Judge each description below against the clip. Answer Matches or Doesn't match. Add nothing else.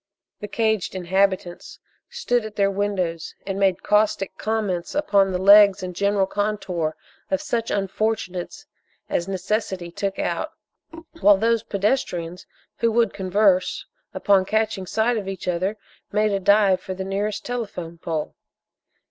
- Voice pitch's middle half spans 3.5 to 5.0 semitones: Doesn't match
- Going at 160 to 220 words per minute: Doesn't match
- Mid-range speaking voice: Doesn't match